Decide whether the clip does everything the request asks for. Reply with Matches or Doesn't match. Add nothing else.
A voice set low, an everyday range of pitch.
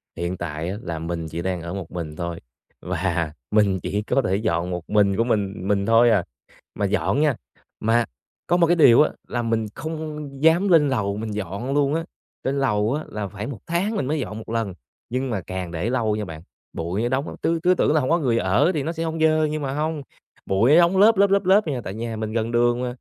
Doesn't match